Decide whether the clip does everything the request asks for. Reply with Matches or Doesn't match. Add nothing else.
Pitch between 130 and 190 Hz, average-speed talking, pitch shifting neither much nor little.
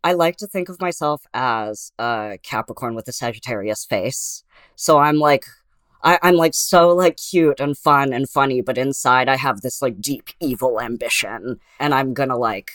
Matches